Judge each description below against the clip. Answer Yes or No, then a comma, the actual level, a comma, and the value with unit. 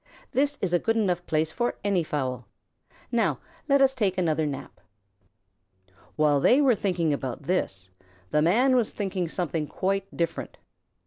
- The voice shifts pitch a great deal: Yes, wide, 6.5 semitones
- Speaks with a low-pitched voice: No, medium, 180 Hz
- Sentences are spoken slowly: No, average, 145 wpm